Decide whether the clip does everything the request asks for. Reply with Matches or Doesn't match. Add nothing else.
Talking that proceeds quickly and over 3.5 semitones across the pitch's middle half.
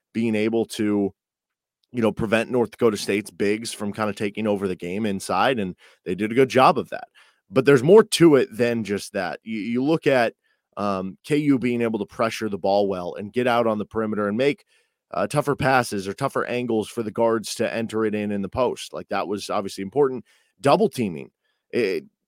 Matches